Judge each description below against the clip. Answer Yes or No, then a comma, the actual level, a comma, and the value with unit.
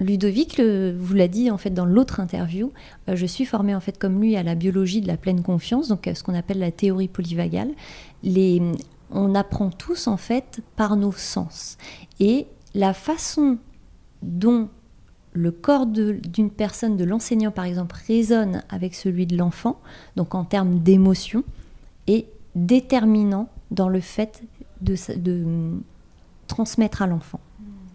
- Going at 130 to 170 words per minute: Yes, average, 160 wpm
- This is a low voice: No, high, 195 Hz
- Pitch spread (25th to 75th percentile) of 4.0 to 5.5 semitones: No, average, 3.5 semitones